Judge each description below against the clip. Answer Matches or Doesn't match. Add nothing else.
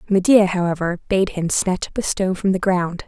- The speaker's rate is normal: Doesn't match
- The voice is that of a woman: Matches